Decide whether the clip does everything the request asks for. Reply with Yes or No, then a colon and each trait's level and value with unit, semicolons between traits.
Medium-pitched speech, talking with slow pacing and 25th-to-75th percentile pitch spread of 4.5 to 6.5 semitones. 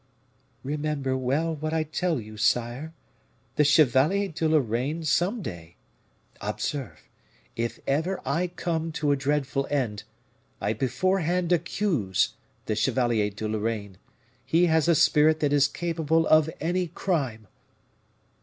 Yes: medium, 150 Hz; slow, 125 wpm; average, 5.1 semitones